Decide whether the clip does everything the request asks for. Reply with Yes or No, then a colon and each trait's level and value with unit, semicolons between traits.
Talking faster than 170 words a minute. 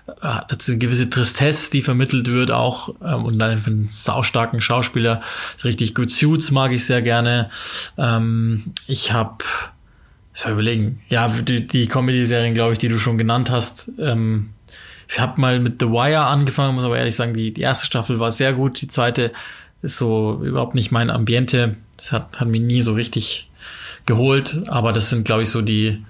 Yes: average, 185 wpm